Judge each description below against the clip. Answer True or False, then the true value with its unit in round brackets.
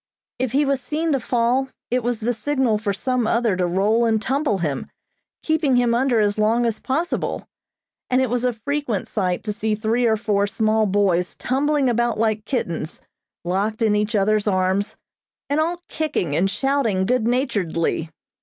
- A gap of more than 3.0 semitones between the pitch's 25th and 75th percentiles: True (4.0 semitones)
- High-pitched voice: True (225 Hz)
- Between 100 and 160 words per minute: False (175 wpm)